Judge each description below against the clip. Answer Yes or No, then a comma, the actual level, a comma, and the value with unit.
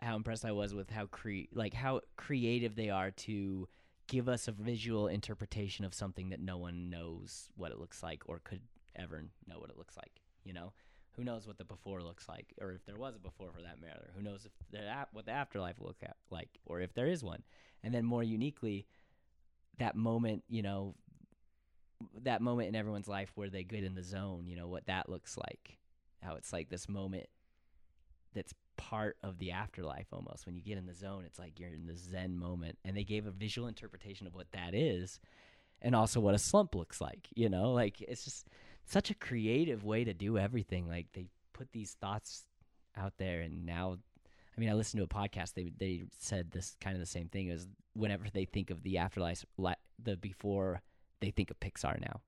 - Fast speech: Yes, fast, 215 wpm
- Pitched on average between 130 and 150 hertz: No, very low, 95 Hz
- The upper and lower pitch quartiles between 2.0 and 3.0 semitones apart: No, average, 3.5 semitones